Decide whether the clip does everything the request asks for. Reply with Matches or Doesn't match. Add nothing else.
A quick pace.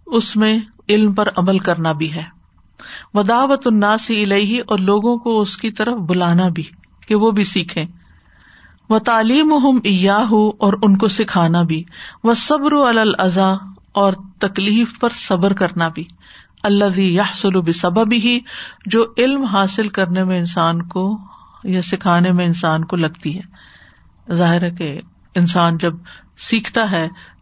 Doesn't match